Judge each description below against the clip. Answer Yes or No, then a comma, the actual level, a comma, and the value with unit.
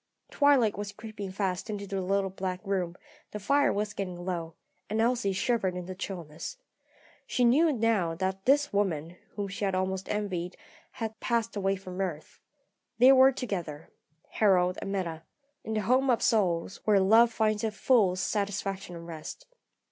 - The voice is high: Yes, high, 200 Hz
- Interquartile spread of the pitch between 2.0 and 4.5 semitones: Yes, average, 3.3 semitones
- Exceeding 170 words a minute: No, average, 165 wpm